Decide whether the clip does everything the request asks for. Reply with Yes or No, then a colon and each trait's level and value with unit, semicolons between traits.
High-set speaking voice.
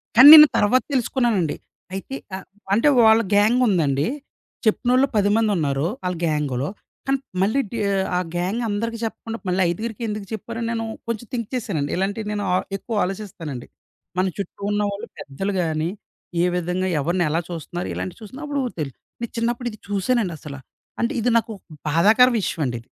Yes: high, 205 Hz